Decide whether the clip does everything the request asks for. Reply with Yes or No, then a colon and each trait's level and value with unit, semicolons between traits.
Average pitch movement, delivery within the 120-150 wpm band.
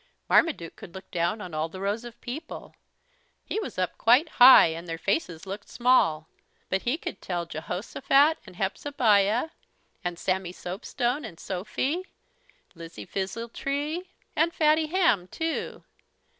No: wide, 8.1 semitones; average, 140 wpm